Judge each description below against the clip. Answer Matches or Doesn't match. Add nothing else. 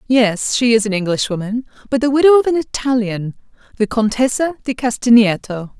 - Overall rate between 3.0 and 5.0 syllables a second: Doesn't match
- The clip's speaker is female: Matches